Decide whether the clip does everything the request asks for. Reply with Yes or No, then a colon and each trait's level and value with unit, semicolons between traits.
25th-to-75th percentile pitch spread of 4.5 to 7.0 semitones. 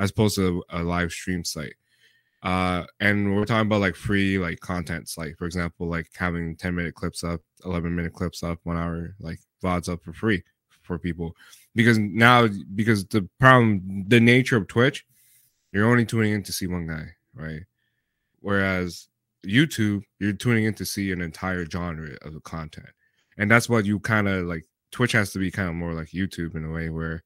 No: average, 4.0 semitones